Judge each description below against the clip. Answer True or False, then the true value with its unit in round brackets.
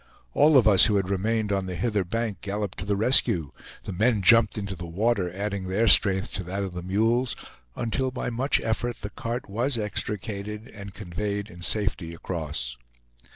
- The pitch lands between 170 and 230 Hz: False (100 Hz)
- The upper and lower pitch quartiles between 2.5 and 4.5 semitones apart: True (3.2 semitones)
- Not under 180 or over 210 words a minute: True (185 wpm)